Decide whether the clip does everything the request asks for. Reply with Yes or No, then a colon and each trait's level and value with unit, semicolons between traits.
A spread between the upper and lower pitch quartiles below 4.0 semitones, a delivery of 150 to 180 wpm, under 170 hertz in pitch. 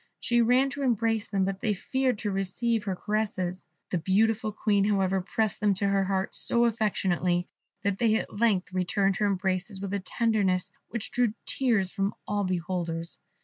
No: average, 2.8 semitones; average, 175 wpm; high, 200 Hz